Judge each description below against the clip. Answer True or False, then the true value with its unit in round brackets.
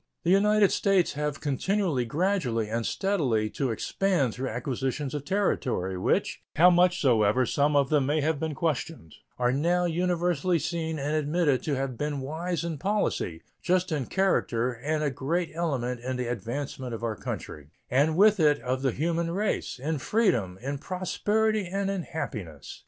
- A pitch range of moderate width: False (5.7 semitones)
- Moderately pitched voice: True (150 Hz)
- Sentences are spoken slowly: False (170 wpm)